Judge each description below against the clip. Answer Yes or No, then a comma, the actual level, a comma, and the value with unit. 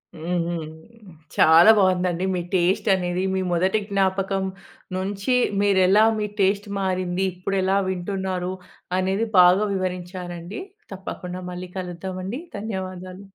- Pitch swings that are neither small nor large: No, narrow, 1.4 semitones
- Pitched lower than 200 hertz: Yes, medium, 185 Hz